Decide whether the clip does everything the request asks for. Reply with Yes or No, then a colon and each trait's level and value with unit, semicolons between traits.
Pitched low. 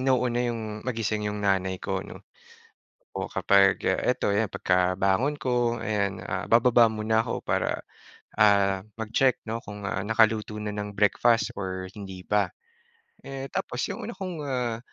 Yes: low, 110 Hz